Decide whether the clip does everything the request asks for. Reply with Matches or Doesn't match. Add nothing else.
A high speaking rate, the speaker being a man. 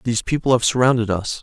Matches